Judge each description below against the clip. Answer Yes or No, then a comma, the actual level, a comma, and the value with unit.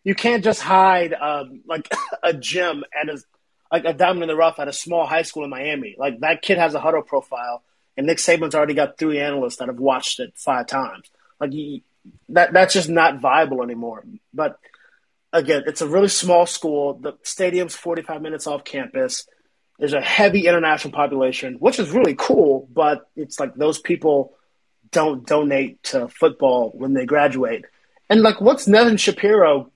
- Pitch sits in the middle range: Yes, medium, 160 Hz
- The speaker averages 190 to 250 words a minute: No, average, 180 wpm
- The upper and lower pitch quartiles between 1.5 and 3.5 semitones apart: No, average, 4.0 semitones